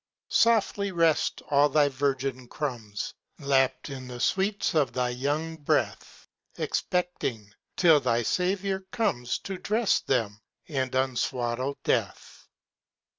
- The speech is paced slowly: Yes, slow, 115 wpm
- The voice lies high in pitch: No, medium, 140 Hz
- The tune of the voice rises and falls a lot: Yes, wide, 5.9 semitones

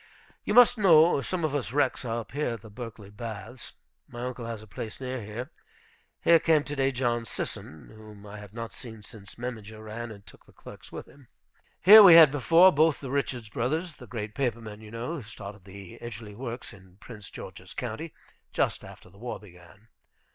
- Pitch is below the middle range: Yes, low, 120 Hz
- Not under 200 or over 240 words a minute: Yes, fast, 205 wpm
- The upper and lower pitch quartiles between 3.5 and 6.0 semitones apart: Yes, average, 4.6 semitones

